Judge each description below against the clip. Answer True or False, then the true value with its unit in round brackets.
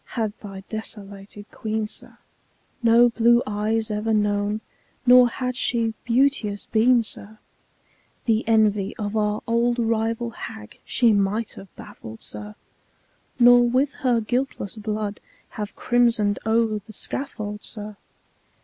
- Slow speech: True (125 wpm)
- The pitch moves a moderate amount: False (2.3 semitones)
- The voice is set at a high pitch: True (220 Hz)